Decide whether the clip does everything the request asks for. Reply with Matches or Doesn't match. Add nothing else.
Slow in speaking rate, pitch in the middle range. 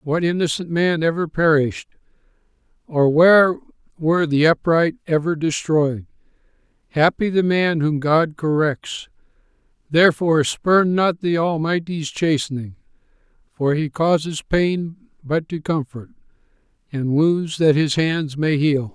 Matches